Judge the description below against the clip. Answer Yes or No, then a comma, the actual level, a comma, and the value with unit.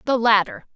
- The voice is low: No, high, 230 Hz